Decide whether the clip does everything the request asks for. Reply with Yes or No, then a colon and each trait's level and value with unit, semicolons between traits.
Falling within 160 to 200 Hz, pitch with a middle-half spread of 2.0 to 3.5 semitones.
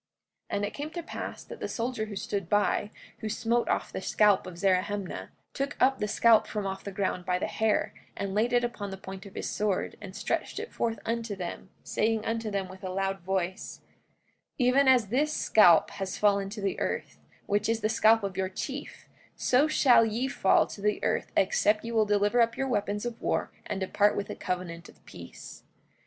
No: high, 210 Hz; average, 3.0 semitones